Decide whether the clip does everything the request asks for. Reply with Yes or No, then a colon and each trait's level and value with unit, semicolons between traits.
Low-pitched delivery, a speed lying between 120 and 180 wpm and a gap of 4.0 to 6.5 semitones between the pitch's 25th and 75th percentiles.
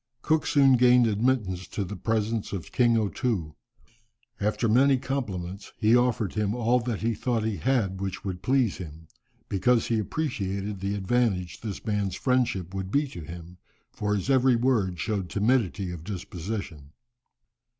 Yes: low, 105 Hz; average, 160 wpm; average, 4.6 semitones